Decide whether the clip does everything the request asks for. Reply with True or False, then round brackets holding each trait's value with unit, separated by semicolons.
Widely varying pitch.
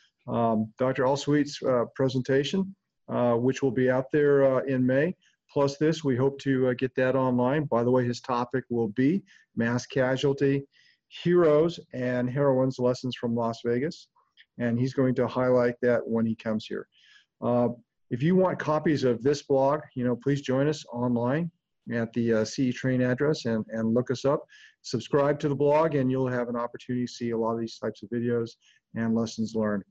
False (2.8 semitones)